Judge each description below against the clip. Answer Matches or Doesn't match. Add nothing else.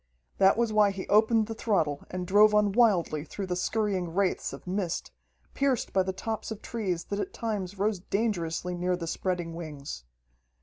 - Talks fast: Doesn't match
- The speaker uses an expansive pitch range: Doesn't match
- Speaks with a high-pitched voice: Matches